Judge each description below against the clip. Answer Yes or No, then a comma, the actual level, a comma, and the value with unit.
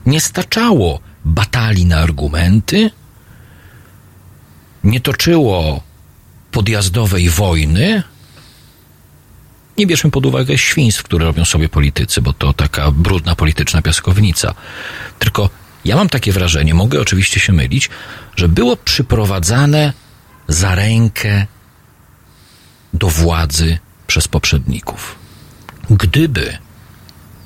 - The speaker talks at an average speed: No, slow, 95 wpm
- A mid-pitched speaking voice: No, very low, 95 Hz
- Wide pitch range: Yes, wide, 5.8 semitones